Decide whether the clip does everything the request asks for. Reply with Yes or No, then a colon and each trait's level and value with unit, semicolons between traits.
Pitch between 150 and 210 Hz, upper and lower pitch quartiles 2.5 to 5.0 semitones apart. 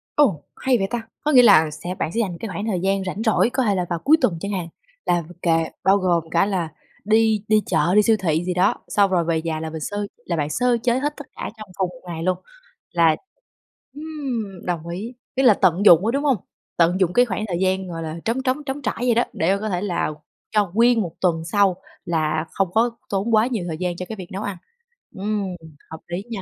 Yes: high, 195 Hz; average, 4.6 semitones